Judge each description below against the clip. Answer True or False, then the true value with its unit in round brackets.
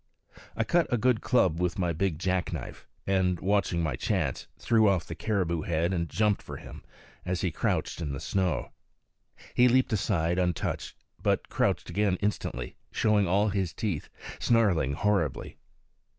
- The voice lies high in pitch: False (95 Hz)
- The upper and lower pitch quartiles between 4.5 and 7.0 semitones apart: False (3.8 semitones)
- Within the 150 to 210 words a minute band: True (160 wpm)